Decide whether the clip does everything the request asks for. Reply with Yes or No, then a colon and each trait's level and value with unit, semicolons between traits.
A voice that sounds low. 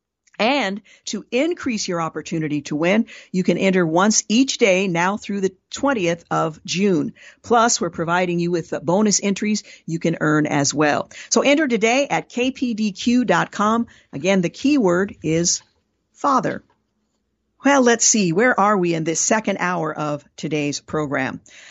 No: high, 190 Hz